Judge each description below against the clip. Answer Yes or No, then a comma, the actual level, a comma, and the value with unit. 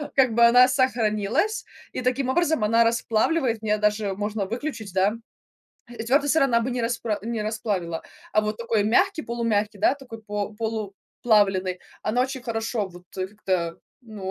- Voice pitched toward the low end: No, high, 225 Hz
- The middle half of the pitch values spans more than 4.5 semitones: No, average, 3.0 semitones